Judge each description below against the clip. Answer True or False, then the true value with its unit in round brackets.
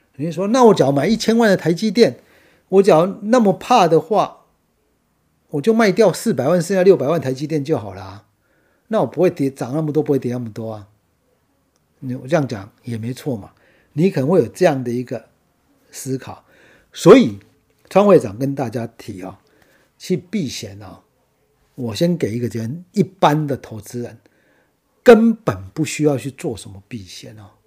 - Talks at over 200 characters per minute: True (260 characters per minute)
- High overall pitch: False (140 Hz)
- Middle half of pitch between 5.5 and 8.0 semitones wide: True (7.6 semitones)